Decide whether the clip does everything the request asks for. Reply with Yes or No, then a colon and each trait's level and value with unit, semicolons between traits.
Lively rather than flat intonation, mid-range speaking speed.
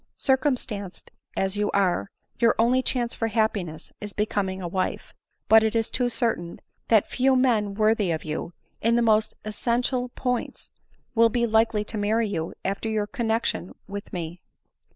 No: average, 2.9 semitones; average, 160 wpm